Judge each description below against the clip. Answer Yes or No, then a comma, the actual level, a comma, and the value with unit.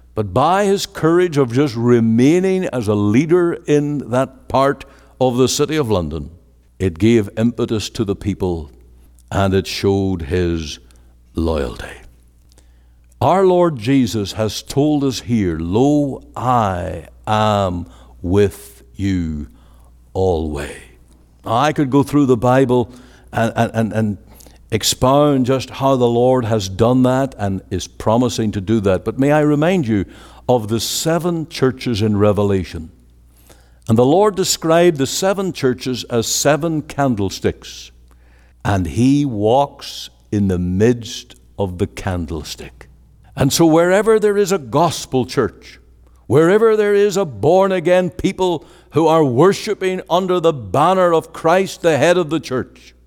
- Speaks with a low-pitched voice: Yes, low, 115 Hz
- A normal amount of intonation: No, wide, 8.4 semitones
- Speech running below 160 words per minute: Yes, average, 140 wpm